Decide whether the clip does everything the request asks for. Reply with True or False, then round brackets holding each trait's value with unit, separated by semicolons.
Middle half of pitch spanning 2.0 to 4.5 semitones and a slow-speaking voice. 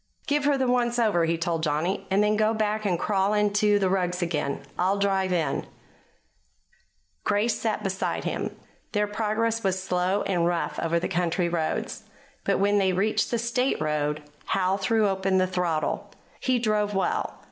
False (3.2 semitones; 170 wpm)